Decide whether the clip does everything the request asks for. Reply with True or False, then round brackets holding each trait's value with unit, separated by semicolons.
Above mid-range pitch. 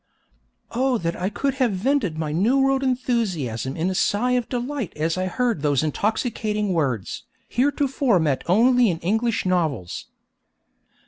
True (210 Hz)